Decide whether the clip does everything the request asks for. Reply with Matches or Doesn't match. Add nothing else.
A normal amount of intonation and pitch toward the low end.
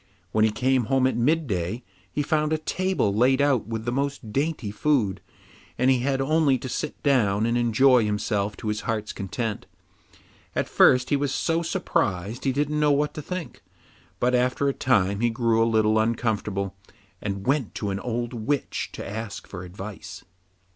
Matches